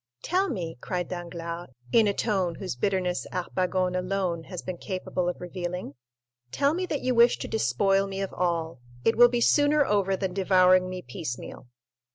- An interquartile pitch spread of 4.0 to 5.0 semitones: No, narrow, 2.6 semitones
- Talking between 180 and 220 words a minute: No, average, 170 wpm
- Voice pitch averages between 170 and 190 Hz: Yes, medium, 185 Hz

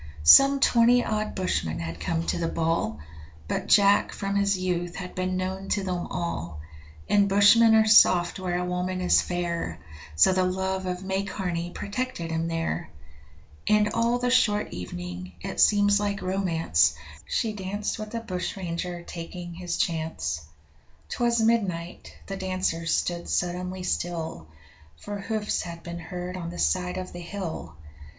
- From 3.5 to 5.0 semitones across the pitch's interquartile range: No, average, 3.1 semitones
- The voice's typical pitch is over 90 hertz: Yes, medium, 185 Hz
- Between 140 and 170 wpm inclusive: Yes, average, 155 wpm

